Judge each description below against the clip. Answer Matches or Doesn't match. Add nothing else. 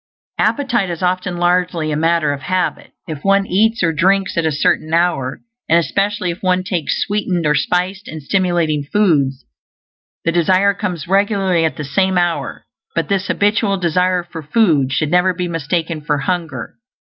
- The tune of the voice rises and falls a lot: Doesn't match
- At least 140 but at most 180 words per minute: Matches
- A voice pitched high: Doesn't match